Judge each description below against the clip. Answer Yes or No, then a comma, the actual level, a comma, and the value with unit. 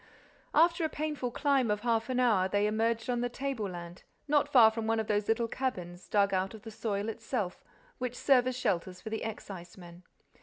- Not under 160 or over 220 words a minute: Yes, average, 195 wpm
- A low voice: No, high, 225 Hz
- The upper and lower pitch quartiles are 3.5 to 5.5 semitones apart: Yes, average, 4.0 semitones